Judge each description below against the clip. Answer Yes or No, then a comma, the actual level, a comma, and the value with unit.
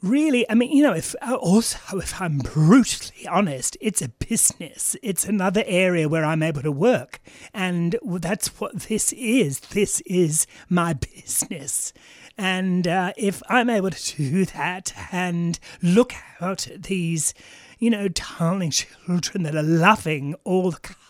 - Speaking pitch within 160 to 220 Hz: Yes, medium, 185 Hz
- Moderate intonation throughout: Yes, average, 4.5 semitones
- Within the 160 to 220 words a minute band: No, average, 150 wpm